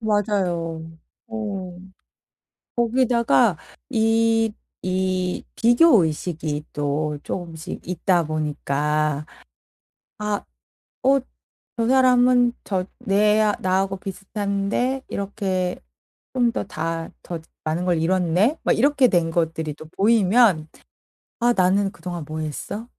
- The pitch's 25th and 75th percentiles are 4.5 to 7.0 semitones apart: Yes, wide, 5.4 semitones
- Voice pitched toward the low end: No, high, 190 Hz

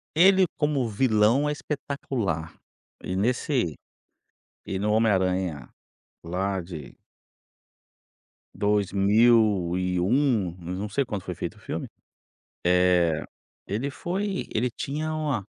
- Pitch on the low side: Yes, low, 105 Hz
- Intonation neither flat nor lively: No, wide, 6.8 semitones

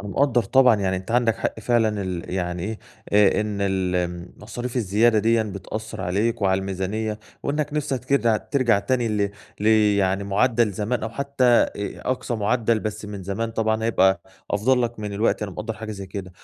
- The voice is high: No, low, 110 Hz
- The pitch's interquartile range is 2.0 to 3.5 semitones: Yes, average, 3.2 semitones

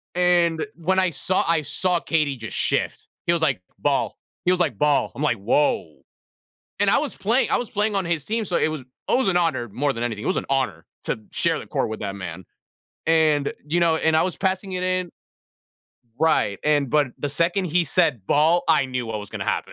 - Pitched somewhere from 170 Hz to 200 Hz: No, medium, 160 Hz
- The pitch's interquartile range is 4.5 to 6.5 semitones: Yes, average, 5.2 semitones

